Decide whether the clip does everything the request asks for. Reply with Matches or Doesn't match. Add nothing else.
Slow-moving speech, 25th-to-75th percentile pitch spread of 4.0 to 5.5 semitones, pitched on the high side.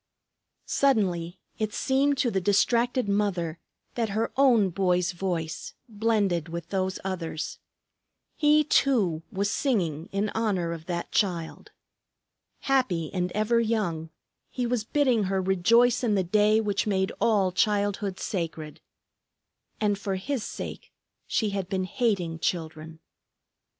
Matches